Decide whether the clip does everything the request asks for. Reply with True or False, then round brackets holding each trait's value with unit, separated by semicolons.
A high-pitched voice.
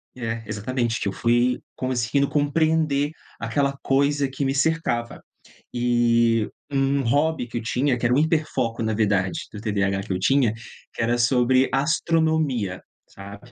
False (125 Hz)